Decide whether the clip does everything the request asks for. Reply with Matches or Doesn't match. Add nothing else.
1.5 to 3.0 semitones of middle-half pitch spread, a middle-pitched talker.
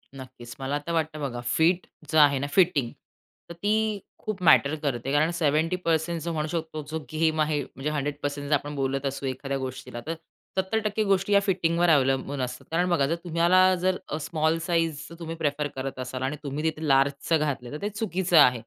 Doesn't match